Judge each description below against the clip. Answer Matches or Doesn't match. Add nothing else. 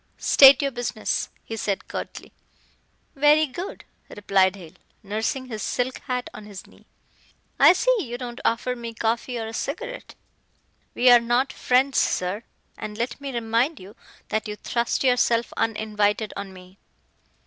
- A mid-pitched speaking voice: Doesn't match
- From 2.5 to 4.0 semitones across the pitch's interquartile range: Matches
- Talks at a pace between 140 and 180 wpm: Matches